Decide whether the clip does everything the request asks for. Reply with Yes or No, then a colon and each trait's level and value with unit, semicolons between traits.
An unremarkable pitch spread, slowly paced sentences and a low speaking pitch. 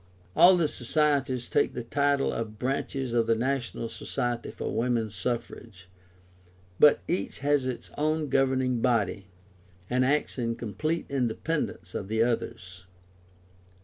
Yes: average, 3.6 semitones; slow, 130 wpm; low, 125 Hz